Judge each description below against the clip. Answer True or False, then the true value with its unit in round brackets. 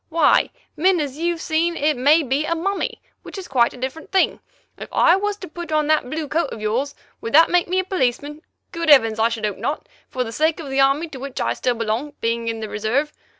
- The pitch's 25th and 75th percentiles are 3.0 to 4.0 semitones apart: False (5.0 semitones)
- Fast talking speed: True (240 wpm)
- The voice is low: False (295 Hz)